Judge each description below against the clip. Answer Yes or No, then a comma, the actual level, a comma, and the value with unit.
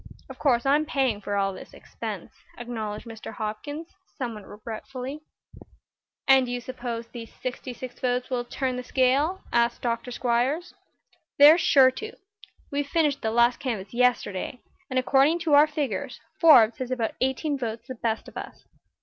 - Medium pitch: No, very high, 250 Hz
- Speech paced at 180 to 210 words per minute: No, average, 160 wpm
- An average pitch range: Yes, average, 3.1 semitones